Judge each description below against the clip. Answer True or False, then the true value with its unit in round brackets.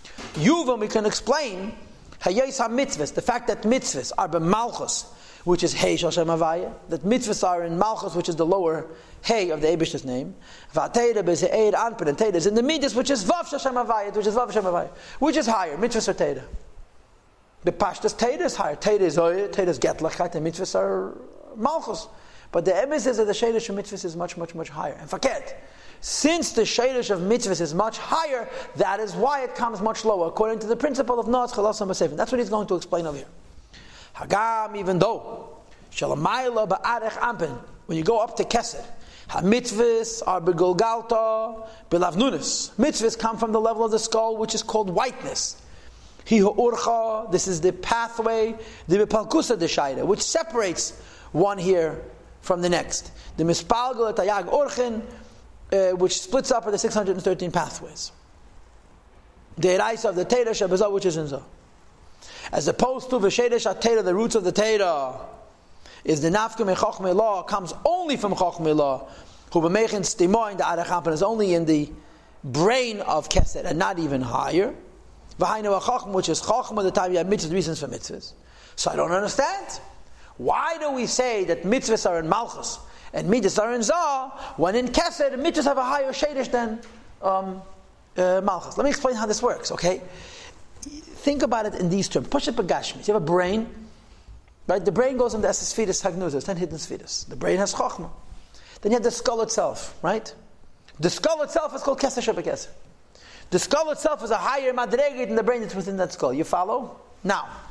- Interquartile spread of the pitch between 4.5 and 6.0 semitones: True (5.1 semitones)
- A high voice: True (215 Hz)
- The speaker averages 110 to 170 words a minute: False (180 wpm)